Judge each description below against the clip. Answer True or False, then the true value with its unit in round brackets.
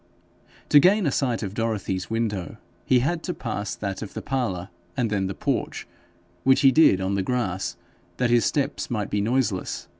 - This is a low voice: True (115 Hz)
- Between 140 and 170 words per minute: False (185 wpm)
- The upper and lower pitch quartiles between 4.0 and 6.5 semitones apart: True (5.2 semitones)